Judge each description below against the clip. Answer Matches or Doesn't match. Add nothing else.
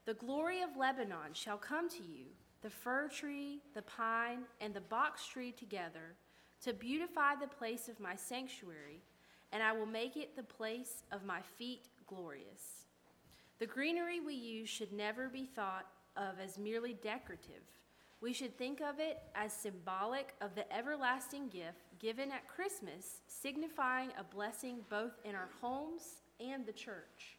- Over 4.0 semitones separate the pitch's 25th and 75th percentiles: Matches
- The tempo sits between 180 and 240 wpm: Doesn't match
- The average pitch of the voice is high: Matches